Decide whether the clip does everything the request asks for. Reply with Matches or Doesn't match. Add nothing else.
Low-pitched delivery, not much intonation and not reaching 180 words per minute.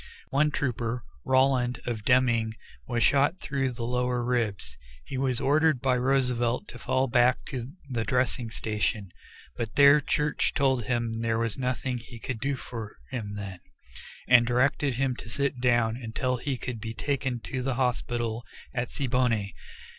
Matches